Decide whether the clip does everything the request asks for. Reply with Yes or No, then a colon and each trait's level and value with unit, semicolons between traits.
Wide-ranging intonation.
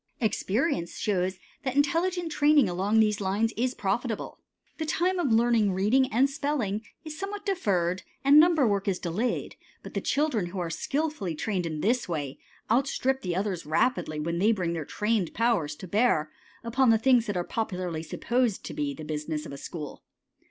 Yes: wide, 6.8 semitones